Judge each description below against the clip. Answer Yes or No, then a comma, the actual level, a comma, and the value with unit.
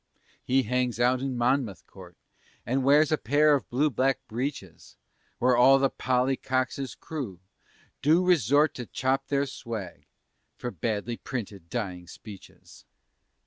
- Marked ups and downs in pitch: No, average, 3.1 semitones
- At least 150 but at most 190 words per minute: No, average, 140 wpm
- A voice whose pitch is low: Yes, low, 125 Hz